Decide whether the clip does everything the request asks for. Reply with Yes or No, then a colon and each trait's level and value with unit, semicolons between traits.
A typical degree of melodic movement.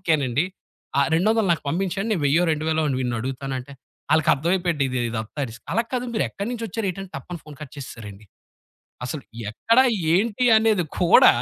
No: wide, 6.4 semitones